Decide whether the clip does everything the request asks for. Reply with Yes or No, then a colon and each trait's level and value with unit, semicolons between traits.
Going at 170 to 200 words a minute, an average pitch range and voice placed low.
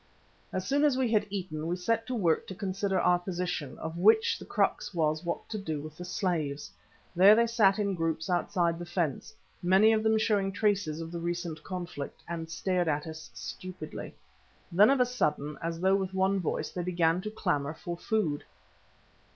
No: average, 190 wpm; average, 3.6 semitones; medium, 180 Hz